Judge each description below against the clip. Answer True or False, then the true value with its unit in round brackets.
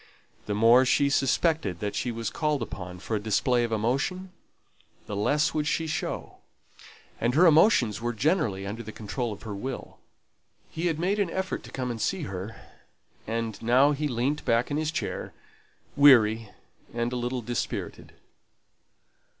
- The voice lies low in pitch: True (125 Hz)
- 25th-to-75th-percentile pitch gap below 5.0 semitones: False (5.3 semitones)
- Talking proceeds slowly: False (165 wpm)